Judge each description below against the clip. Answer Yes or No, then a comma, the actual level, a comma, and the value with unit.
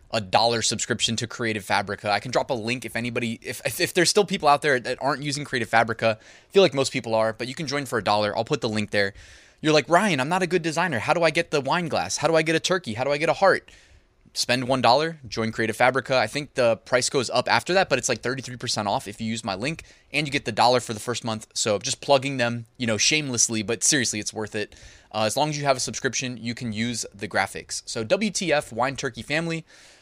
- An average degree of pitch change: Yes, average, 4.4 semitones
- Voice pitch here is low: Yes, low, 120 Hz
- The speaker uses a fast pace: Yes, fast, 265 wpm